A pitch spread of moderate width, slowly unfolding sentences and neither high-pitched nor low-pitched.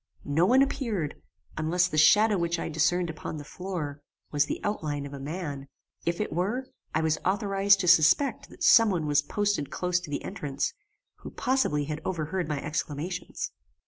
No: average, 4.7 semitones; average, 175 wpm; medium, 170 Hz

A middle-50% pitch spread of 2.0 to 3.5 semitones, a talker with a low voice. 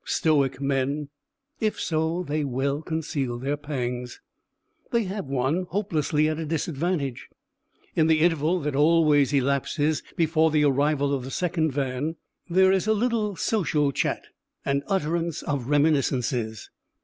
No: average, 3.1 semitones; medium, 150 Hz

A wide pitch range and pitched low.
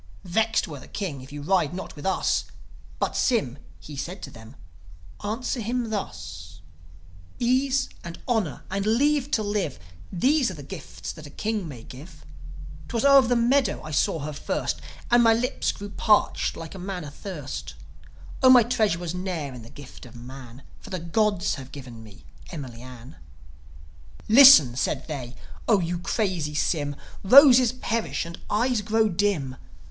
No: wide, 8.0 semitones; medium, 180 Hz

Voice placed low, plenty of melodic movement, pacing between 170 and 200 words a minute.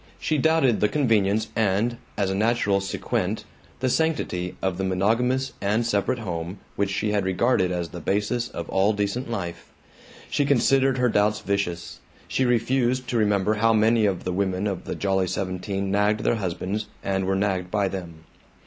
No: low, 105 Hz; average, 3.6 semitones; average, 175 wpm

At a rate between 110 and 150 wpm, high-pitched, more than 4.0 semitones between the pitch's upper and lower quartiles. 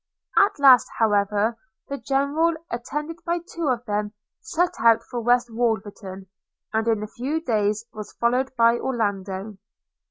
Yes: average, 145 wpm; high, 235 Hz; average, 4.6 semitones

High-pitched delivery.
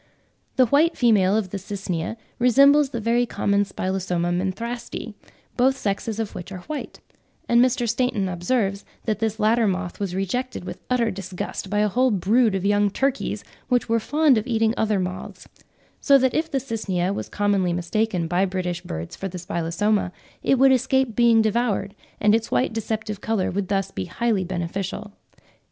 Yes: high, 210 Hz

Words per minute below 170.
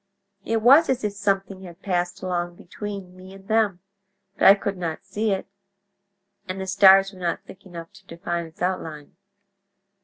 No: average, 175 wpm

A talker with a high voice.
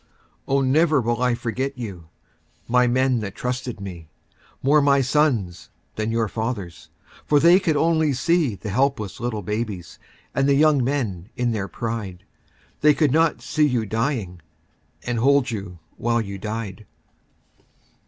No: low, 120 Hz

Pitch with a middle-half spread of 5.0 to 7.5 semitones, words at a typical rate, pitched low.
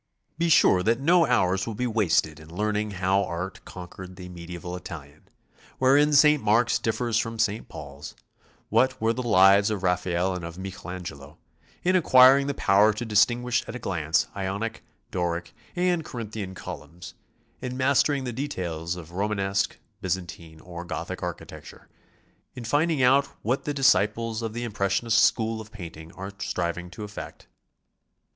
Yes: wide, 5.4 semitones; average, 155 wpm; low, 105 Hz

